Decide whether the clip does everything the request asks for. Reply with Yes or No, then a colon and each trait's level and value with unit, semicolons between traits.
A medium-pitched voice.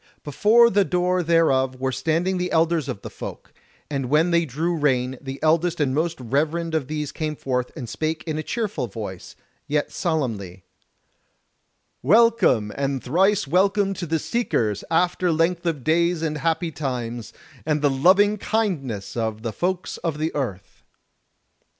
Yes: medium, 155 Hz